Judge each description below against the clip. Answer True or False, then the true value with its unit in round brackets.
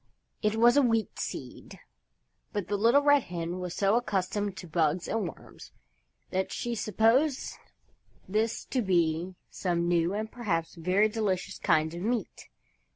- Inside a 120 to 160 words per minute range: True (150 wpm)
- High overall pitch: True (200 Hz)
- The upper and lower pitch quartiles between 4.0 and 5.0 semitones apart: True (4.4 semitones)